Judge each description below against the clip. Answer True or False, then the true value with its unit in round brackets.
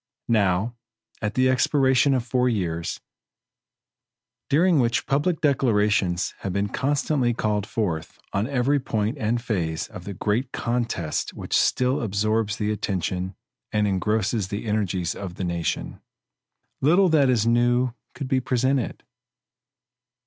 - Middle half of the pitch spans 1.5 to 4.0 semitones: False (4.5 semitones)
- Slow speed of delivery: True (130 wpm)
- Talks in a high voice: False (115 Hz)